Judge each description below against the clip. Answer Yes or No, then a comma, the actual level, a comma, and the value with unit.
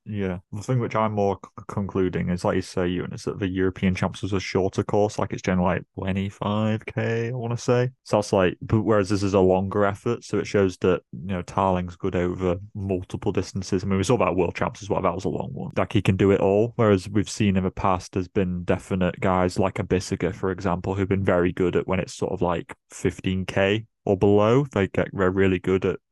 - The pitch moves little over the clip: Yes, narrow, 2.1 semitones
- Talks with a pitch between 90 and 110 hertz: Yes, very low, 95 Hz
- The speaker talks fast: Yes, fast, 245 wpm